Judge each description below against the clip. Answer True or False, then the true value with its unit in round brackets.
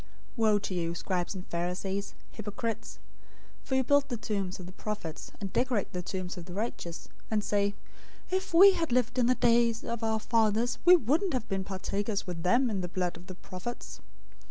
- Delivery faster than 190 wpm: True (205 wpm)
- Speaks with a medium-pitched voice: False (210 Hz)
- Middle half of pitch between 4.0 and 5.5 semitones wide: True (4.6 semitones)